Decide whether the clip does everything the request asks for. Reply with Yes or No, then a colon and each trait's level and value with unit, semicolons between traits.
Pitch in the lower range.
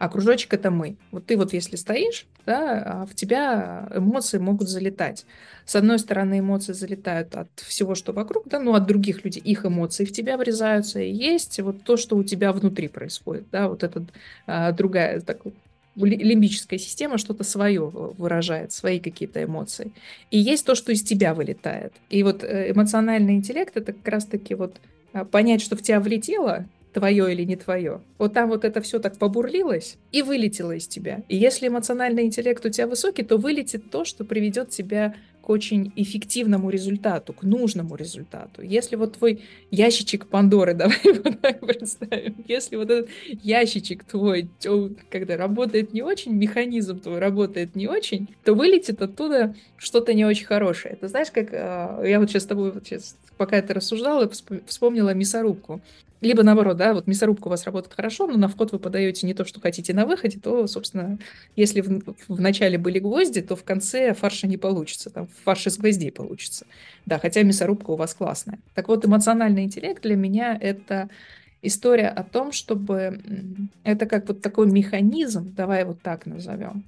No: high, 205 Hz